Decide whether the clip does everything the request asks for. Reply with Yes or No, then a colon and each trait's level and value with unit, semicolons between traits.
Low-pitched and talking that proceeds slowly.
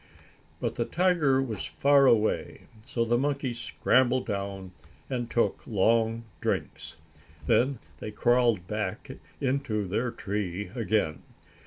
Yes: low, 115 Hz; slow, 120 wpm